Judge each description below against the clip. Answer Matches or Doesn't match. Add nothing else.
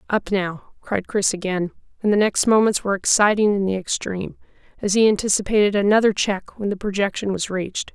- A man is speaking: Doesn't match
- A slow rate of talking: Doesn't match